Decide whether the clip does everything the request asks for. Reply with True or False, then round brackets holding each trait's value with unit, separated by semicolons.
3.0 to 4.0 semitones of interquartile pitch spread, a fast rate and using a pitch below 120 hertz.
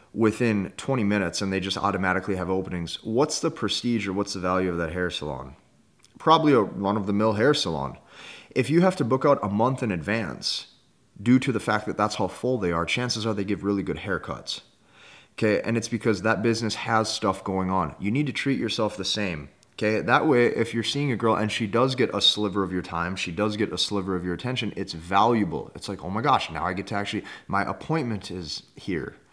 True (3.5 semitones; 230 wpm; 105 Hz)